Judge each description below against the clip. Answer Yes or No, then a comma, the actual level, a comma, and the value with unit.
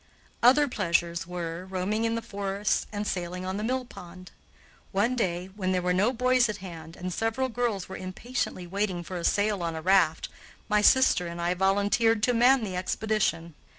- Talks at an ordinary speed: Yes, average, 185 wpm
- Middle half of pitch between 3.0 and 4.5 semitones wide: Yes, average, 4.0 semitones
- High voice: Yes, high, 195 Hz